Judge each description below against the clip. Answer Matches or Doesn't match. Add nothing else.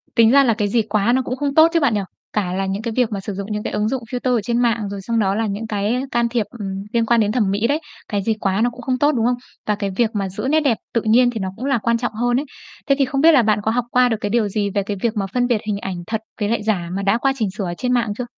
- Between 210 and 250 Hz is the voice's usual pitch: Matches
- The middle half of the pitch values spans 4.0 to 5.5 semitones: Doesn't match